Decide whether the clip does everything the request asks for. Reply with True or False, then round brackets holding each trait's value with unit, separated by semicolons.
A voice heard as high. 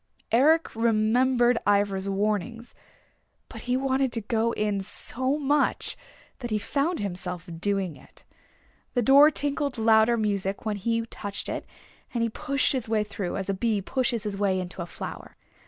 True (225 Hz)